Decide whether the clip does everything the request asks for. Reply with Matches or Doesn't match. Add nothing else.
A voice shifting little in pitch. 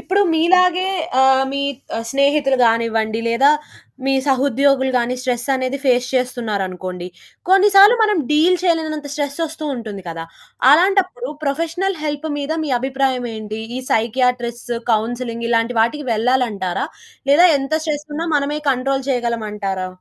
Doesn't match